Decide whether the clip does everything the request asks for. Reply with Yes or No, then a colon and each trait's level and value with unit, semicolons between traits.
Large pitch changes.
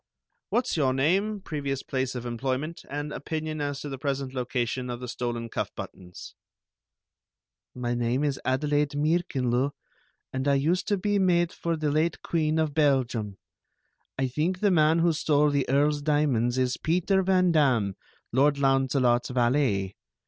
No: average, 3.7 semitones